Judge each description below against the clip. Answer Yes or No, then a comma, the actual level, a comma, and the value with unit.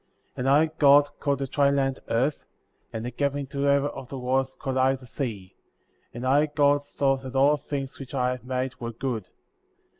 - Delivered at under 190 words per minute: No, average, 200 wpm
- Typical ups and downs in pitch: No, narrow, 1.8 semitones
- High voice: No, low, 135 Hz